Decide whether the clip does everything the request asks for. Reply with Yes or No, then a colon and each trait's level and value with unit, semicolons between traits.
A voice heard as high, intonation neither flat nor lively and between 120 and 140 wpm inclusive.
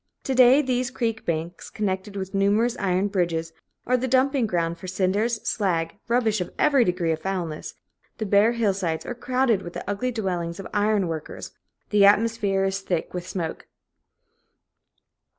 No: high, 200 Hz; average, 4.4 semitones; average, 160 wpm